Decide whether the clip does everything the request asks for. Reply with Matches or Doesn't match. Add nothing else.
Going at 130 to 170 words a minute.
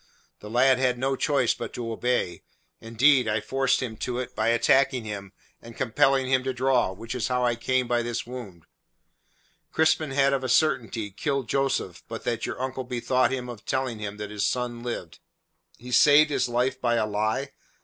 Doesn't match